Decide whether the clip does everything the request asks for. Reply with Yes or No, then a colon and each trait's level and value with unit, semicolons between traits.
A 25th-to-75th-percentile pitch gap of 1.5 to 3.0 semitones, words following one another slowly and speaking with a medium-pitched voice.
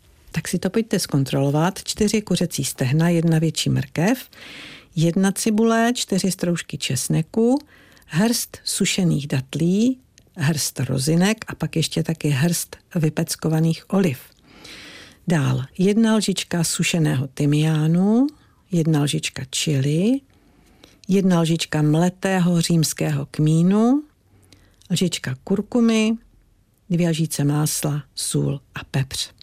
No: average, 4.8 semitones; slow, 100 wpm; medium, 165 Hz